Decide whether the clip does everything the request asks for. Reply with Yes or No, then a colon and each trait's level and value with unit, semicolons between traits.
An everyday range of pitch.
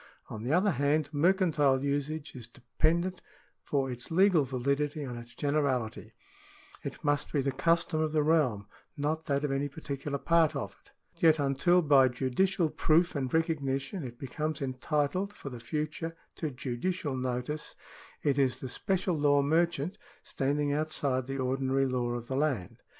Yes: average, 3.2 semitones